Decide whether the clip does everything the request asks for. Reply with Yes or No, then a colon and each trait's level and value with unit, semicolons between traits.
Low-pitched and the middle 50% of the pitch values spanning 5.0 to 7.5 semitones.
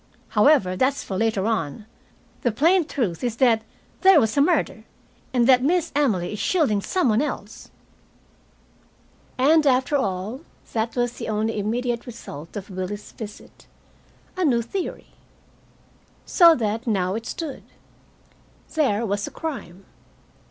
No: high, 235 Hz; wide, 5.4 semitones